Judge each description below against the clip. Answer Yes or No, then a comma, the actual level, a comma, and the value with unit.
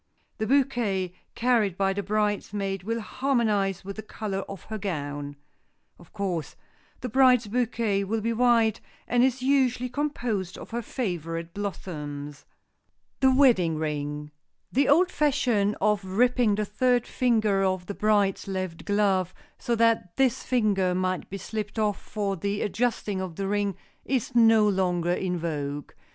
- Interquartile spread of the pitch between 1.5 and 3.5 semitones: No, average, 4.1 semitones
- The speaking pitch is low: No, high, 205 Hz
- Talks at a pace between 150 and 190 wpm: Yes, average, 155 wpm